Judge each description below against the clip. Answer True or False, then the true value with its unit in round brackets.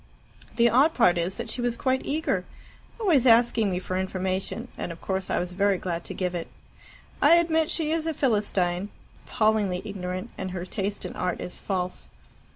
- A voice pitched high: True (200 Hz)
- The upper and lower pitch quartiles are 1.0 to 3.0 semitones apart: False (5.3 semitones)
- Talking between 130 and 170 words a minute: False (185 wpm)